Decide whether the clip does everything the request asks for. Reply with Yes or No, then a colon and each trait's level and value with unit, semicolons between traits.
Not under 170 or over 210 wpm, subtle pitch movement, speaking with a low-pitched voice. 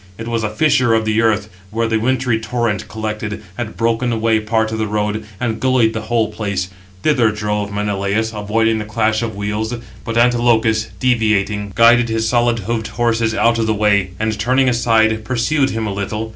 Yes: average, 185 wpm; narrow, 1.6 semitones; low, 110 Hz